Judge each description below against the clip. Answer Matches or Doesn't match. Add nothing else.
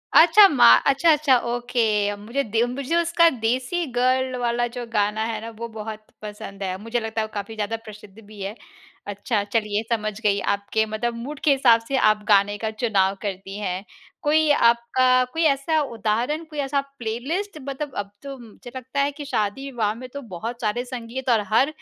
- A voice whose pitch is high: Matches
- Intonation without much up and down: Doesn't match